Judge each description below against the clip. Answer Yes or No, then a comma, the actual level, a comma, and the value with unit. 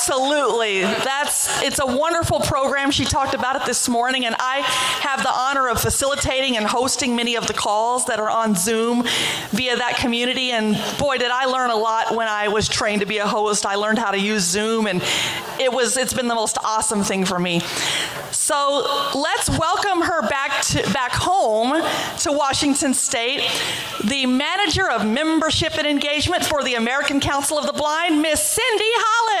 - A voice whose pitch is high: Yes, very high, 255 Hz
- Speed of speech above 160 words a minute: Yes, average, 185 wpm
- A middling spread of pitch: Yes, average, 4.3 semitones